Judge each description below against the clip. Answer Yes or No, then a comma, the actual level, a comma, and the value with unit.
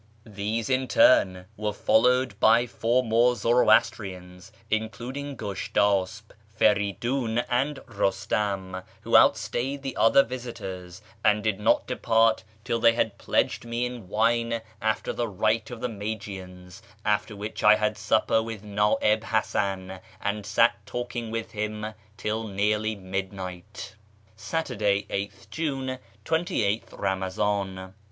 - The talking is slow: Yes, slow, 125 wpm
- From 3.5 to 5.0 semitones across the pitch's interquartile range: No, average, 2.8 semitones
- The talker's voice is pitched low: Yes, low, 110 Hz